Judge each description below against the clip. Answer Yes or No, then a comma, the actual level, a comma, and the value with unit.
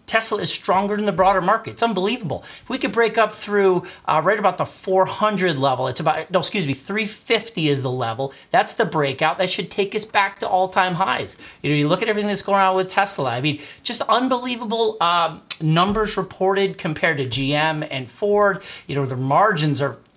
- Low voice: No, high, 190 Hz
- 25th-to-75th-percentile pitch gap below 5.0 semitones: No, average, 5.3 semitones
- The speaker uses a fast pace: Yes, fast, 210 wpm